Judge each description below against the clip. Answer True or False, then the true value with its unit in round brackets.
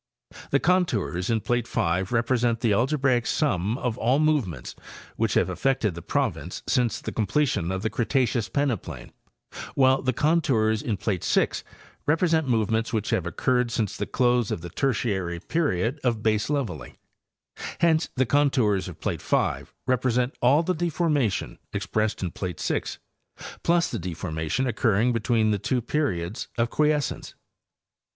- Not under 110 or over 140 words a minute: False (150 wpm)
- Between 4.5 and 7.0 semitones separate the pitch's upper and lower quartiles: True (5.2 semitones)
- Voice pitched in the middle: False (120 Hz)